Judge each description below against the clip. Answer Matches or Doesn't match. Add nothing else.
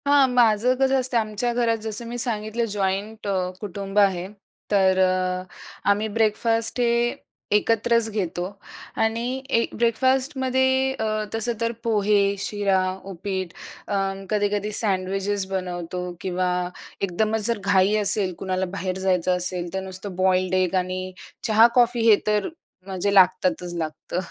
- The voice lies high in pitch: Matches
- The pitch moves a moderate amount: Matches